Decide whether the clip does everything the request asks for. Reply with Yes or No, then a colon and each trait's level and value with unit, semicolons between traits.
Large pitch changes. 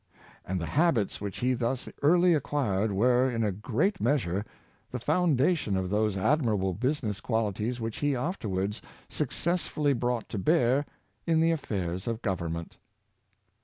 Yes: wide, 6.4 semitones